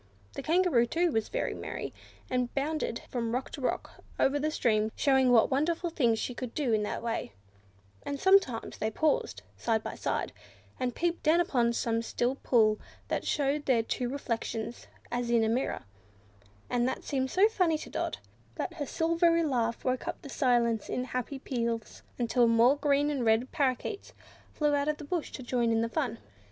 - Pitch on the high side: Yes, very high, 255 Hz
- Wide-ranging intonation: No, average, 4.3 semitones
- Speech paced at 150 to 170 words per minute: No, average, 185 wpm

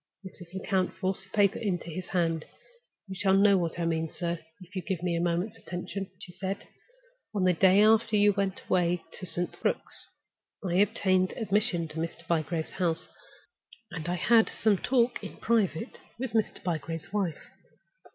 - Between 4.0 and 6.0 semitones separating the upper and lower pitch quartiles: No, average, 2.8 semitones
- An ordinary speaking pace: Yes, average, 175 wpm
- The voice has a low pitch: No, medium, 185 Hz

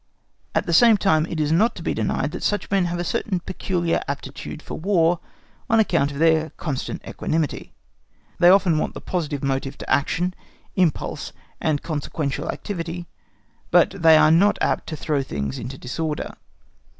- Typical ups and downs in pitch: Yes, average, 3.5 semitones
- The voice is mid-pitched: Yes, medium, 165 Hz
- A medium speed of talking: Yes, average, 170 wpm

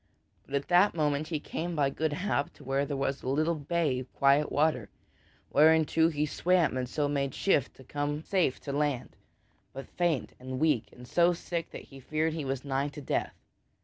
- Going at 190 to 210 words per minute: Yes, average, 200 wpm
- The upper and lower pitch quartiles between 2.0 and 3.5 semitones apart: Yes, average, 2.9 semitones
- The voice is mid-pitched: Yes, medium, 145 Hz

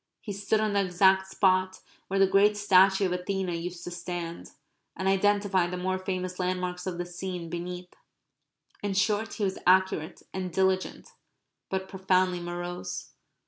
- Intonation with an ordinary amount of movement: No, narrow, 1.3 semitones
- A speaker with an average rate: Yes, average, 155 wpm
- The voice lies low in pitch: No, medium, 185 Hz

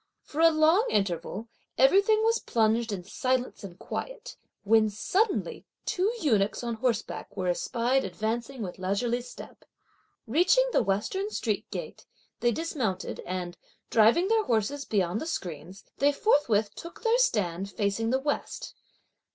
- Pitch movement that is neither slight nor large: No, wide, 8.2 semitones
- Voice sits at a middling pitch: No, high, 235 Hz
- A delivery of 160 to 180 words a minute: No, average, 140 wpm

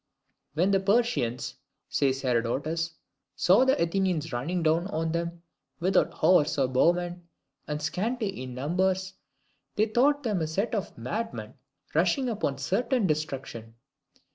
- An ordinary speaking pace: No, slow, 130 wpm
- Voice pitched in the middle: Yes, medium, 170 Hz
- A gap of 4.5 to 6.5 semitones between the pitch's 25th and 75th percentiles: Yes, average, 5.2 semitones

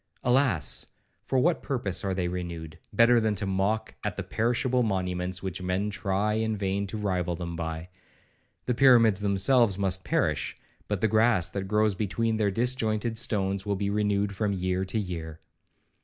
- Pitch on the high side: No, low, 100 Hz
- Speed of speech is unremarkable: Yes, average, 170 wpm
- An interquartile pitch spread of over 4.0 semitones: No, average, 3.2 semitones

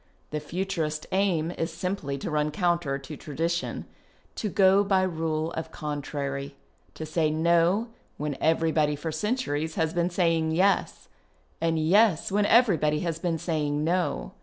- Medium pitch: Yes, medium, 165 Hz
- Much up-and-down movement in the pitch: No, average, 3.1 semitones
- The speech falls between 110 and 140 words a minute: No, average, 150 wpm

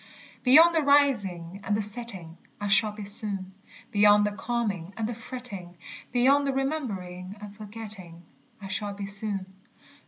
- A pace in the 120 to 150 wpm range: Yes, average, 145 wpm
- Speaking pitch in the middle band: No, high, 205 Hz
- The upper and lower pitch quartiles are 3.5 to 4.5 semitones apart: Yes, average, 3.8 semitones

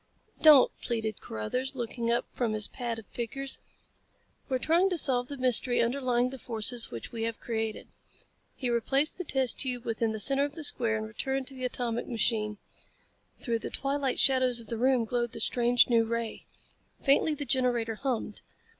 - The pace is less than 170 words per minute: No, average, 180 wpm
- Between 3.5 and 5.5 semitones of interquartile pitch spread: No, average, 2.7 semitones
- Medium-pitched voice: No, high, 245 Hz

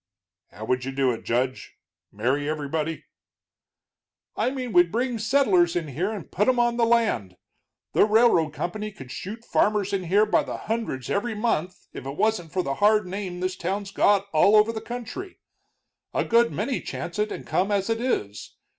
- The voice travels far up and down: Yes, wide, 6.2 semitones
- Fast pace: No, average, 185 wpm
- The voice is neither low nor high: No, high, 200 Hz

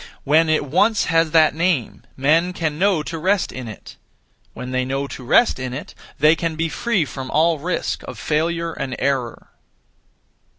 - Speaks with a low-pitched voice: No, medium, 155 Hz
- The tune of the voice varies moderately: Yes, average, 3.6 semitones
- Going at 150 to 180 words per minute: Yes, average, 175 wpm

